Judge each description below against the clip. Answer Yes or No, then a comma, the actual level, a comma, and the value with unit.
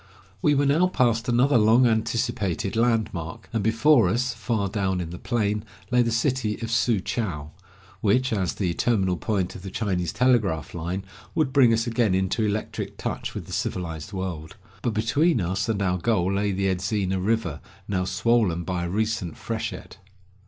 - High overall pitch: No, low, 105 Hz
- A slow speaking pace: No, average, 175 wpm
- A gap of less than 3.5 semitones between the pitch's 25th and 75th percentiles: No, average, 4.1 semitones